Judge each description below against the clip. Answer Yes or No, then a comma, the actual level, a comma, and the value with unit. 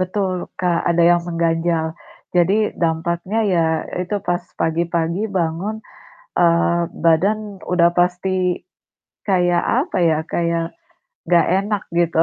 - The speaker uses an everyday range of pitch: No, narrow, 1.8 semitones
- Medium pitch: Yes, medium, 175 Hz